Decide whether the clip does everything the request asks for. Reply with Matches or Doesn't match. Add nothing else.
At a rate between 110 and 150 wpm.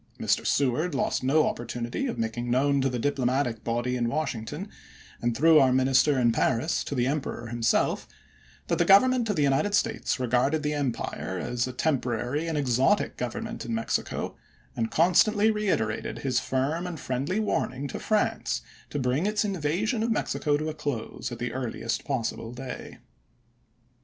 Doesn't match